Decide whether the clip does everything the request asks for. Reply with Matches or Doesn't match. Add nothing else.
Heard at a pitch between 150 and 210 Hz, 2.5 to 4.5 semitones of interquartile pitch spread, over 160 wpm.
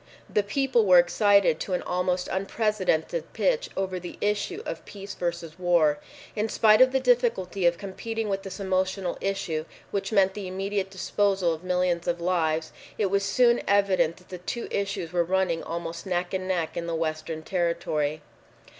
Matches